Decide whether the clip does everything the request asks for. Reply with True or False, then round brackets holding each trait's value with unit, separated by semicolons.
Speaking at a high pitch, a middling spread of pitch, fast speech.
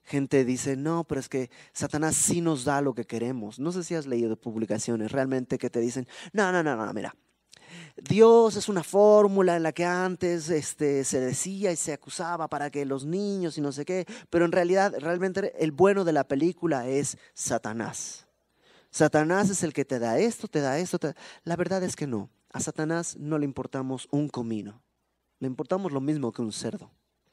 False (155 Hz; 5.0 semitones; 200 wpm)